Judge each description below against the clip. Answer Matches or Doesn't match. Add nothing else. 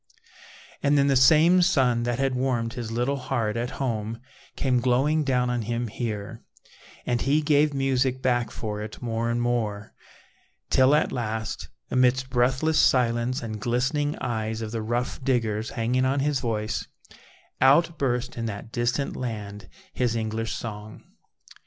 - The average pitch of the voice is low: Matches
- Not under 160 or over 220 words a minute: Doesn't match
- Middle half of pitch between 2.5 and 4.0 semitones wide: Matches